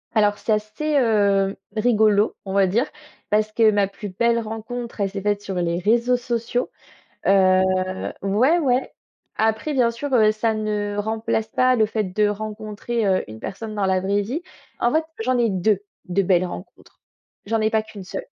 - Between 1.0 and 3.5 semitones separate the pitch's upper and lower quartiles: Yes, average, 2.7 semitones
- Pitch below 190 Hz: No, high, 215 Hz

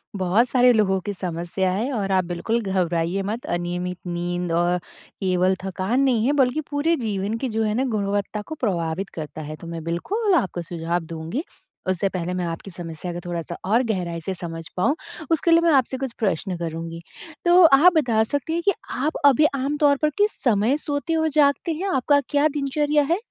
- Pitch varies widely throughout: Yes, wide, 8.2 semitones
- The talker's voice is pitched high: Yes, high, 205 Hz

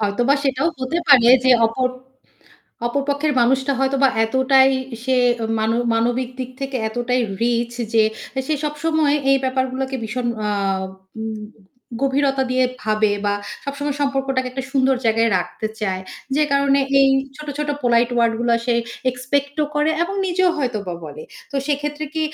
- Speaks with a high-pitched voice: Yes, very high, 260 Hz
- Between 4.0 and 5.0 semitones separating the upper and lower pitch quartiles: No, average, 3.0 semitones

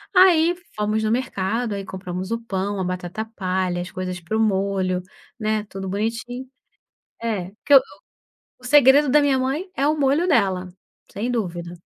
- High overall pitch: Yes, high, 215 Hz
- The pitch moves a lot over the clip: Yes, wide, 5.7 semitones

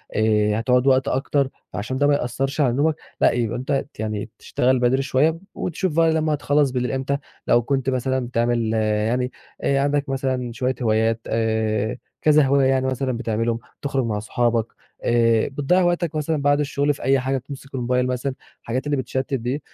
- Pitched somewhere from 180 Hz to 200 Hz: No, low, 130 Hz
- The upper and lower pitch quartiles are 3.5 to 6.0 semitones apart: No, average, 3.0 semitones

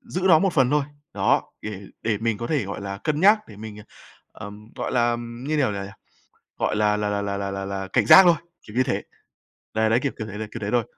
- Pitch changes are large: No, average, 4.3 semitones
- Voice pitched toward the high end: No, low, 110 Hz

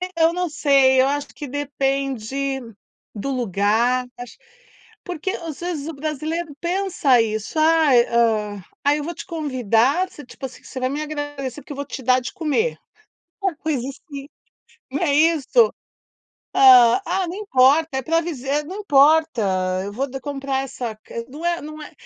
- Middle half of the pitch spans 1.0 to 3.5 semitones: No, average, 4.0 semitones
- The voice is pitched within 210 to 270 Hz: No, very high, 280 Hz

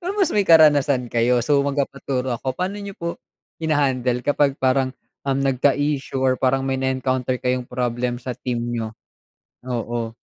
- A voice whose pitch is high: No, low, 130 Hz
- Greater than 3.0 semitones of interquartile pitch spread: No, narrow, 2.4 semitones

